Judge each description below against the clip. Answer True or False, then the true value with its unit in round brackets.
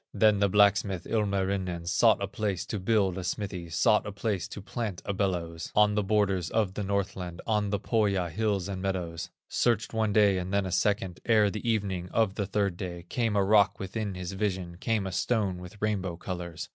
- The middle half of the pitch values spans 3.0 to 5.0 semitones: False (2.5 semitones)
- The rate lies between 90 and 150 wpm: False (200 wpm)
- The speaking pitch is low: True (100 Hz)